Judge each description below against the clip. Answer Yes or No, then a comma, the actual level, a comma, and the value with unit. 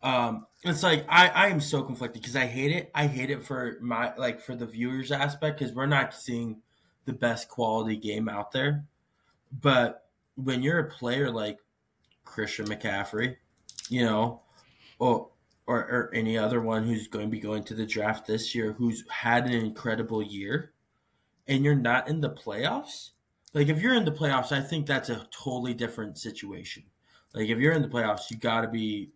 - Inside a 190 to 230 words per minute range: Yes, average, 200 wpm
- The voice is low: Yes, low, 120 Hz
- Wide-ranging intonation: No, average, 4.1 semitones